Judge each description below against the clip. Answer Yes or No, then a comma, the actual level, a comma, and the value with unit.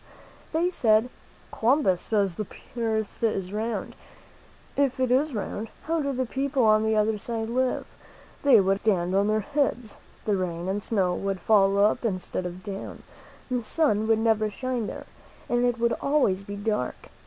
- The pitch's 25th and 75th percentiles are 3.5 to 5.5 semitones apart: Yes, average, 3.8 semitones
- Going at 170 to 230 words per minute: Yes, average, 180 wpm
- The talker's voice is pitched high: Yes, high, 220 Hz